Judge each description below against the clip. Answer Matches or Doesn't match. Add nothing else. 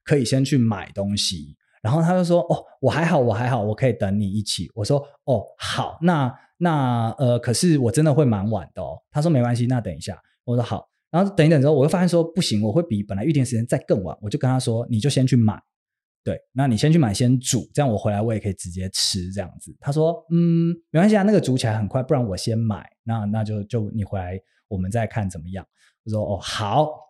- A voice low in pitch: Matches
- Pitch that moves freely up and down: Matches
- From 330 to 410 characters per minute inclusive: Matches